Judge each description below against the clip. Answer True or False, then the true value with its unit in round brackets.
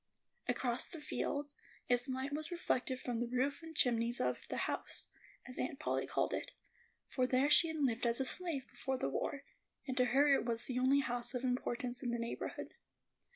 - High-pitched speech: True (255 Hz)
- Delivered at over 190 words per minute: True (200 wpm)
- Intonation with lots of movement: False (2.6 semitones)